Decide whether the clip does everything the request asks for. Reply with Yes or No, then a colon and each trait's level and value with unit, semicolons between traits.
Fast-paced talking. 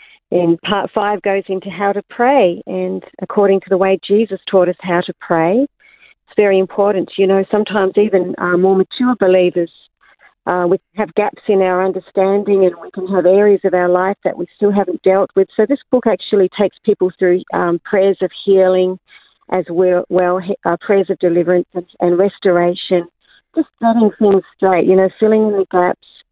No: average, 185 wpm